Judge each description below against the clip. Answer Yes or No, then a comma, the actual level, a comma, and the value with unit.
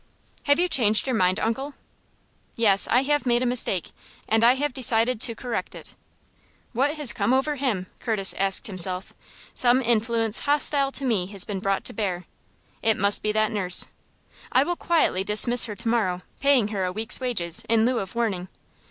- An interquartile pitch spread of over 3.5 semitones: Yes, average, 4.4 semitones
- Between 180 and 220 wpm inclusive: Yes, average, 185 wpm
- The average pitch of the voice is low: No, high, 225 Hz